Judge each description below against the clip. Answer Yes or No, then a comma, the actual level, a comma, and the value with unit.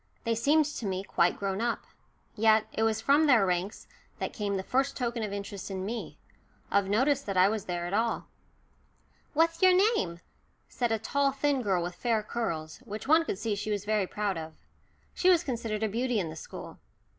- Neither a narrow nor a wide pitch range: Yes, average, 4.6 semitones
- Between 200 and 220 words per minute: Yes, fast, 205 wpm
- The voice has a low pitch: No, high, 220 Hz